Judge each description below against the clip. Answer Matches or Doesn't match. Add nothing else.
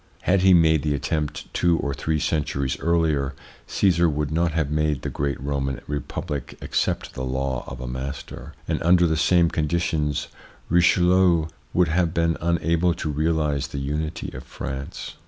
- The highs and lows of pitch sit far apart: Doesn't match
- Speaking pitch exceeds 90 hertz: Doesn't match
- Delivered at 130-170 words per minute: Matches